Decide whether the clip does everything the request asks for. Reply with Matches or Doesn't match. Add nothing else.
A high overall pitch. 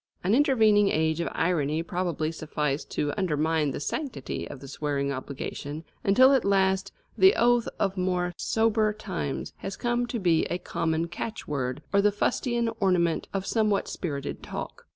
Doesn't match